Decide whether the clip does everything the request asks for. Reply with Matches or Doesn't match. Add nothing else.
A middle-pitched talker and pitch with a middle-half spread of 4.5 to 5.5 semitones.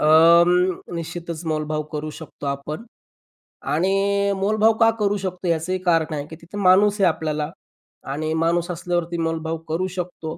Doesn't match